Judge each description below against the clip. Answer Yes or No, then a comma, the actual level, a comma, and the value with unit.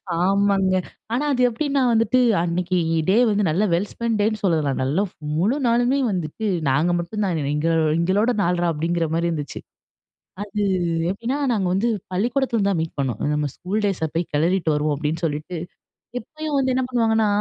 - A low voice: No, high, 190 Hz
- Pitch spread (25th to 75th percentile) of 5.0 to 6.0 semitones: Yes, wide, 5.4 semitones